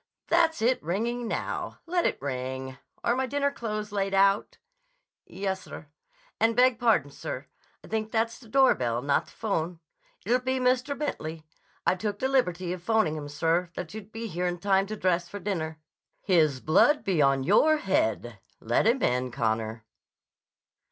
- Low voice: No, high, 195 Hz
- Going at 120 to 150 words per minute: No, average, 165 wpm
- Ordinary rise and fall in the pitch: No, wide, 7.1 semitones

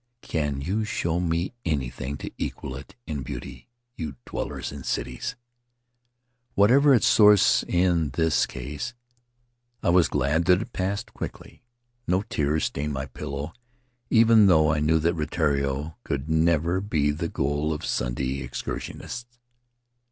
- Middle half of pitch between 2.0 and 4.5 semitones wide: No, wide, 5.6 semitones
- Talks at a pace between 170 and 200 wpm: No, average, 140 wpm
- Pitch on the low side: Yes, very low, 80 Hz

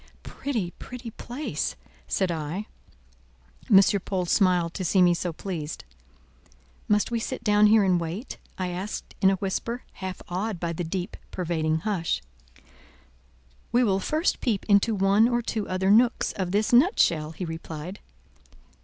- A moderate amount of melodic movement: Yes, average, 3.7 semitones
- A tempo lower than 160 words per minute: Yes, average, 150 wpm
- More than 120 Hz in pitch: Yes, high, 190 Hz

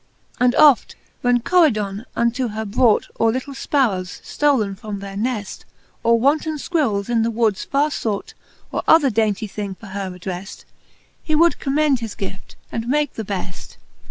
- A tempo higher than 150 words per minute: Yes, average, 160 wpm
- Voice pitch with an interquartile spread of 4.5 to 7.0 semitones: Yes, average, 5.3 semitones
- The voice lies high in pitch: Yes, high, 230 Hz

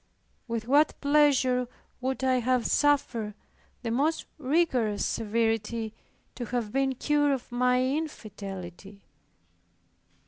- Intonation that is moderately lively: Yes, average, 3.7 semitones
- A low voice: No, very high, 250 Hz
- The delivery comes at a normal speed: No, slow, 105 wpm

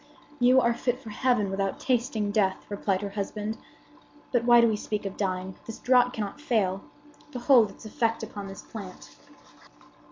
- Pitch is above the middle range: Yes, high, 215 Hz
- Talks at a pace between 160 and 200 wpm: Yes, average, 165 wpm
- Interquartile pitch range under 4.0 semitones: Yes, average, 3.5 semitones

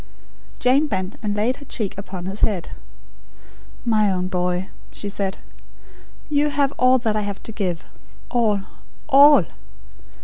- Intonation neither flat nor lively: Yes, average, 4.9 semitones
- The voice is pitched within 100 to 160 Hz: No, high, 210 Hz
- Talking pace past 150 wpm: No, slow, 135 wpm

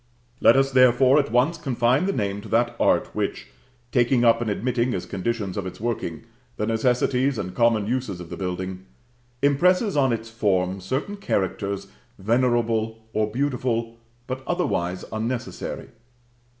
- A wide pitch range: No, average, 4.0 semitones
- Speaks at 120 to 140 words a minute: No, average, 150 wpm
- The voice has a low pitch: Yes, low, 115 Hz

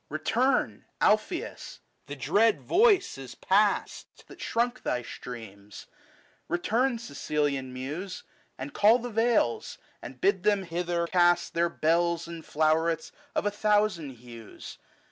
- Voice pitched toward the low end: No, medium, 170 Hz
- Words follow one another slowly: Yes, slow, 125 wpm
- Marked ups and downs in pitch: Yes, wide, 7.0 semitones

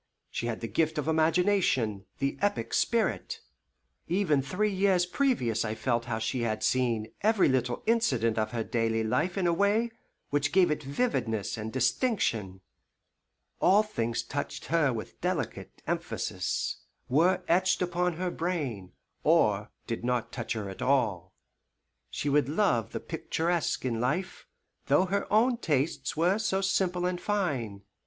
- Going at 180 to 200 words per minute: No, average, 150 wpm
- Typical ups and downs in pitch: No, wide, 8.1 semitones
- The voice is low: No, medium, 145 Hz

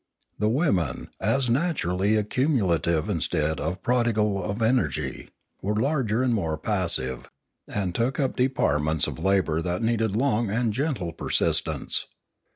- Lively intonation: Yes, wide, 5.8 semitones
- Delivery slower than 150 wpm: Yes, slow, 135 wpm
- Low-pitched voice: Yes, low, 105 Hz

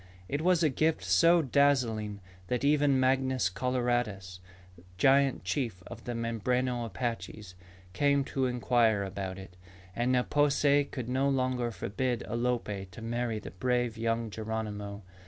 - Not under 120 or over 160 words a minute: Yes, average, 140 wpm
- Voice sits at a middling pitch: No, low, 120 Hz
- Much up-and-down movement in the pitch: No, average, 3.6 semitones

